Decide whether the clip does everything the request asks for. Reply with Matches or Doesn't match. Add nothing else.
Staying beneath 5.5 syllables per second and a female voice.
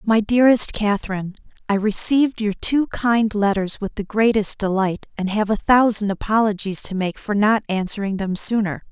Matches